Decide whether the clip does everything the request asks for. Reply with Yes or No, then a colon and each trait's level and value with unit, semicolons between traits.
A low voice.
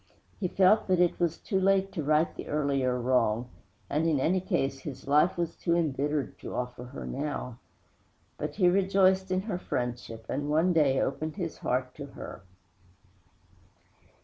No: medium, 150 Hz